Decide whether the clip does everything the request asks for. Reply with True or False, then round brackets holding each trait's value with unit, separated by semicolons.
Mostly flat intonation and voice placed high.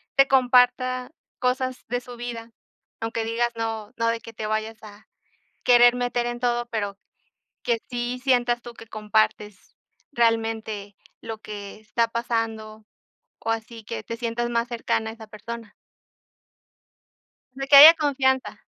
True (1.9 semitones; 230 Hz)